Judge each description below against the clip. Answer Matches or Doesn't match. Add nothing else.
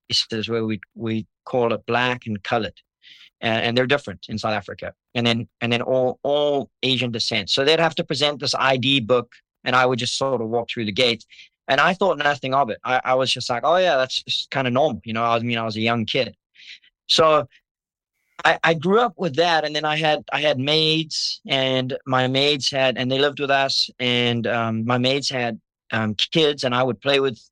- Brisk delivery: Matches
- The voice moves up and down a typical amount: Matches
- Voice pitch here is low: Matches